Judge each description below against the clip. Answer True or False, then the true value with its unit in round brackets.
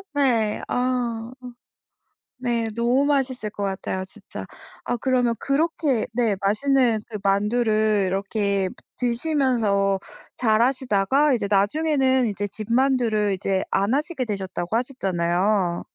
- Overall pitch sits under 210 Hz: False (230 Hz)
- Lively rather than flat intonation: False (4.5 semitones)